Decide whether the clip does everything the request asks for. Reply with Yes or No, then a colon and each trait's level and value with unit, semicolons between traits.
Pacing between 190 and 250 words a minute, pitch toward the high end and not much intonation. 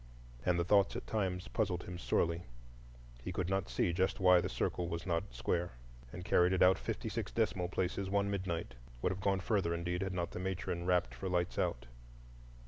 No: average, 195 wpm; very low, 90 Hz; narrow, 1.8 semitones